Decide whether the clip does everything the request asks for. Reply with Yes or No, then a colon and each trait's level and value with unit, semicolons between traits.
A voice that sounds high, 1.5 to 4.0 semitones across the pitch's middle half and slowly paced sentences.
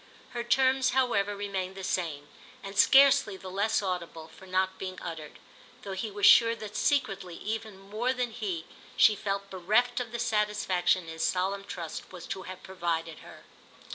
No: high, 195 Hz; average, 3.1 semitones; average, 170 wpm